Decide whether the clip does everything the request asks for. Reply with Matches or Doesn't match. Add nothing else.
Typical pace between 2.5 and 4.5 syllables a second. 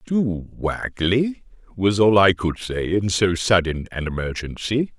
Matches